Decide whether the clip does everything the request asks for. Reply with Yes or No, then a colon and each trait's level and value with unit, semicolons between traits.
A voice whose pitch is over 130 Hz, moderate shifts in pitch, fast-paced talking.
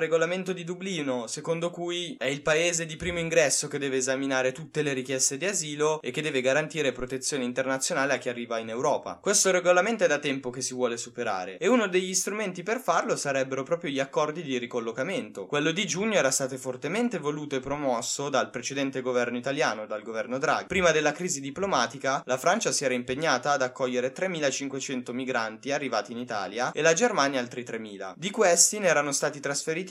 Yes: medium, 140 Hz; average, 4.8 semitones; fast, 190 wpm